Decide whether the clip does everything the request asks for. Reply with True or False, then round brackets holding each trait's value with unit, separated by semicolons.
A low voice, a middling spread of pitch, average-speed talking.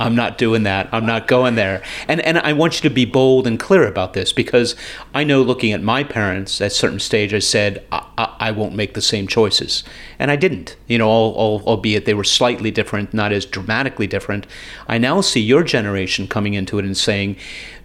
False (110 Hz; 3.4 semitones; 225 wpm)